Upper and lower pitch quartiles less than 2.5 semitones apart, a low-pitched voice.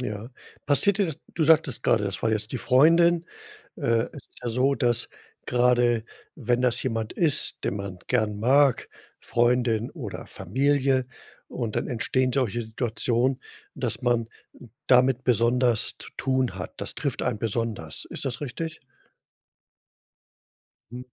No: average, 2.8 semitones; low, 125 Hz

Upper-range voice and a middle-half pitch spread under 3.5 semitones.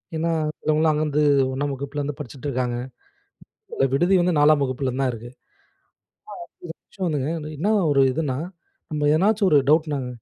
No: medium, 150 Hz; average, 2.7 semitones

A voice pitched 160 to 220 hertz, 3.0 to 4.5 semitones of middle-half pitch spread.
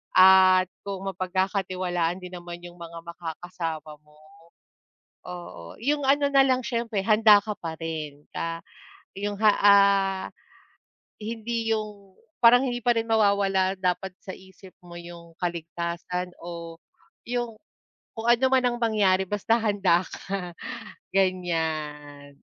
Yes: high, 190 Hz; average, 3.9 semitones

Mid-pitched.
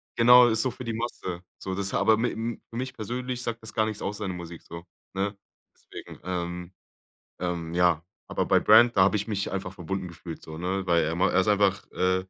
No: very low, 95 Hz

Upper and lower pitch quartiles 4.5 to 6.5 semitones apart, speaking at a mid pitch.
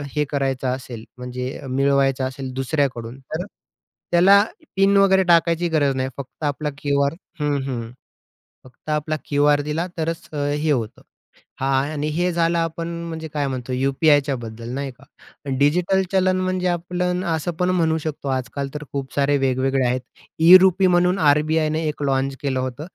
No: average, 3.8 semitones; medium, 145 Hz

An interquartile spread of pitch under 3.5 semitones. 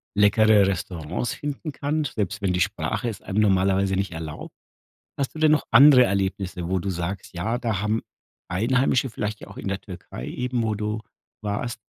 No: average, 4.1 semitones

